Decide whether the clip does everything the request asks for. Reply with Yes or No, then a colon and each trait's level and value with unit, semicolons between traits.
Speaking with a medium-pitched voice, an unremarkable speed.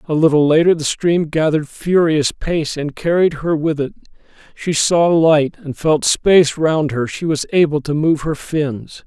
Yes: medium, 155 Hz; average, 185 wpm